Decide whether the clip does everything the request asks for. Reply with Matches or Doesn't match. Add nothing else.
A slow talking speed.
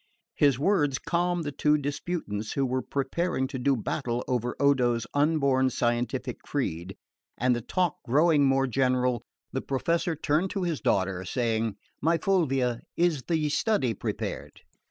Doesn't match